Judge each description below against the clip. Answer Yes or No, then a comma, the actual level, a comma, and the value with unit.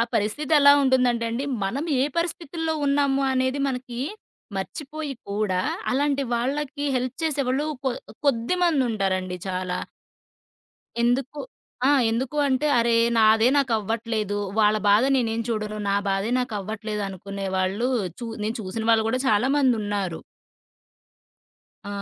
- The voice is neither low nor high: No, high, 235 Hz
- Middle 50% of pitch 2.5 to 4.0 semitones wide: No, average, 4.5 semitones